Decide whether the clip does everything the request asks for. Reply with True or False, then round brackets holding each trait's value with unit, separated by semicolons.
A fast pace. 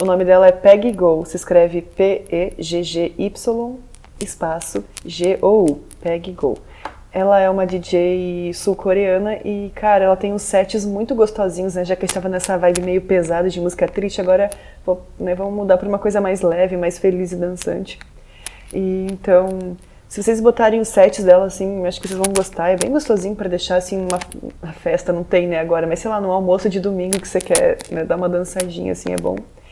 True (195 wpm)